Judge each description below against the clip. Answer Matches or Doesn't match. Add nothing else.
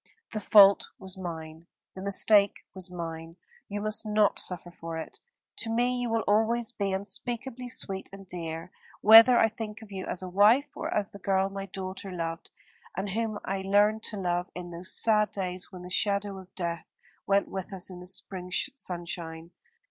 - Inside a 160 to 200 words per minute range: Matches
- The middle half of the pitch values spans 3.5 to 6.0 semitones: Doesn't match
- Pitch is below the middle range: Doesn't match